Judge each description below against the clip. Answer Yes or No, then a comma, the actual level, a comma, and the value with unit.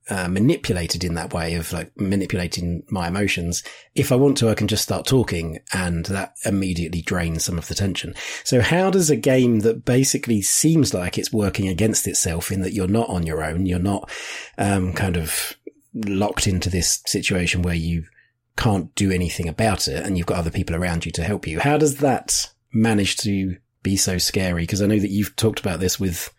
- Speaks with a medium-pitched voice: No, very low, 95 Hz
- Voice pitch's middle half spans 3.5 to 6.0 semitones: Yes, average, 3.8 semitones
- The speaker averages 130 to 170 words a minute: No, fast, 205 wpm